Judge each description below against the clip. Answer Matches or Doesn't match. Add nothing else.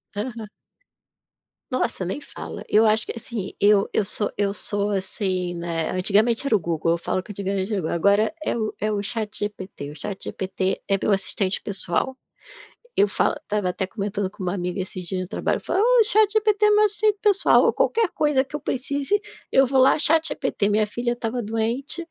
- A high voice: Matches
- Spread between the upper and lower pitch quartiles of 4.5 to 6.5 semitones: Matches